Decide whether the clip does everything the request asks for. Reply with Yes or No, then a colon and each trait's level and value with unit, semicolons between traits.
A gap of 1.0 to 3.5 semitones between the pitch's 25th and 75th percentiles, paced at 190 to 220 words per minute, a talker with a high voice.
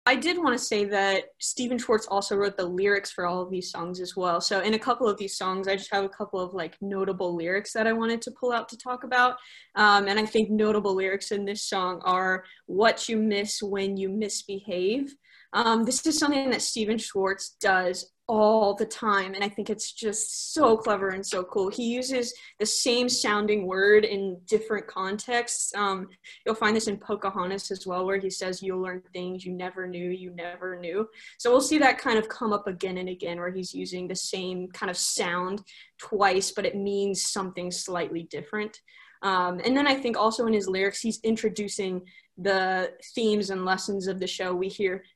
Yes: average, 2.8 semitones; fast, 205 wpm; high, 200 Hz